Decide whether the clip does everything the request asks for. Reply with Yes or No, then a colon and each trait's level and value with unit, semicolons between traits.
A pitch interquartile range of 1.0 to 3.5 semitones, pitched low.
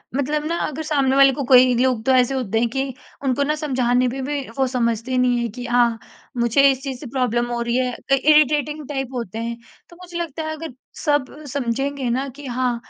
No: average, 2.9 semitones; very high, 260 Hz